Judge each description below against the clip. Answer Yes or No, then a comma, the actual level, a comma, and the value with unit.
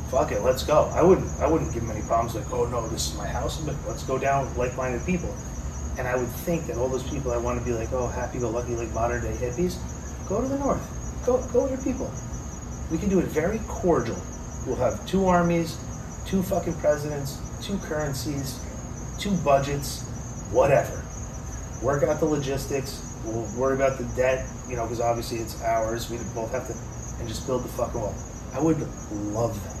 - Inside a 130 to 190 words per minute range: No, fast, 205 wpm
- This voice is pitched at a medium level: No, low, 125 Hz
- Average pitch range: Yes, average, 3.4 semitones